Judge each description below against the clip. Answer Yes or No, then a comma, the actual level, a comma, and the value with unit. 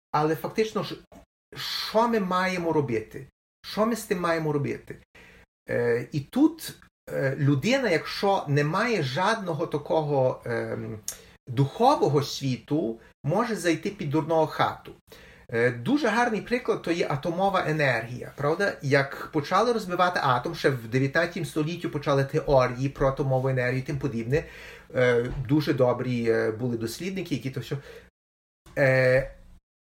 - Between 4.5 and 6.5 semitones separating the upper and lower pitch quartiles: Yes, average, 5.2 semitones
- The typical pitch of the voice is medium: Yes, medium, 150 Hz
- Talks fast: No, average, 115 wpm